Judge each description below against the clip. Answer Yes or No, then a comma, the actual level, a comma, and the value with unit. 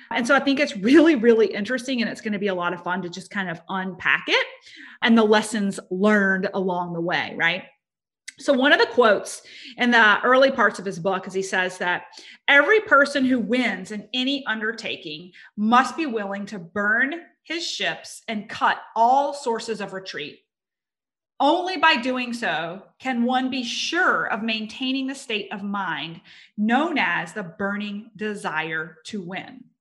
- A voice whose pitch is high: Yes, high, 225 Hz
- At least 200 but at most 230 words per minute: No, average, 175 wpm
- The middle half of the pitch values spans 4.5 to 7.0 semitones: Yes, average, 5.3 semitones